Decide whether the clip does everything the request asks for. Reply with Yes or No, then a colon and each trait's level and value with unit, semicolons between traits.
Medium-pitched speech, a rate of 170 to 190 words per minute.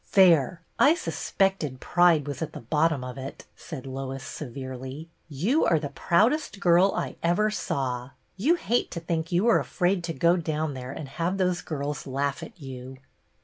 Yes: medium, 160 Hz; average, 180 wpm